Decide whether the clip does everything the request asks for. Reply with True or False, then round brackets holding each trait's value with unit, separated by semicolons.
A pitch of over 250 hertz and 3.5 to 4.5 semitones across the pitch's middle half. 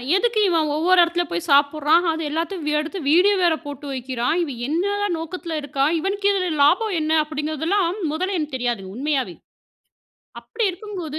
True (320 Hz; 4.1 semitones)